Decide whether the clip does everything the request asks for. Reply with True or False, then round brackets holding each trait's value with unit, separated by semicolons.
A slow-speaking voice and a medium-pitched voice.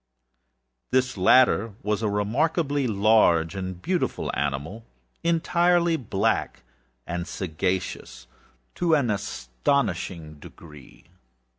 False (90 wpm; 105 Hz)